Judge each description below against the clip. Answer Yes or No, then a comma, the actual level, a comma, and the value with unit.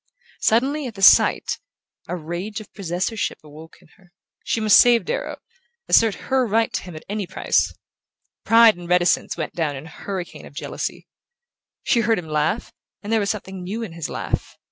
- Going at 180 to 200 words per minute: Yes, average, 185 wpm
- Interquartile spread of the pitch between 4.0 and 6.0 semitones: Yes, average, 4.6 semitones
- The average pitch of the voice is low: No, high, 195 Hz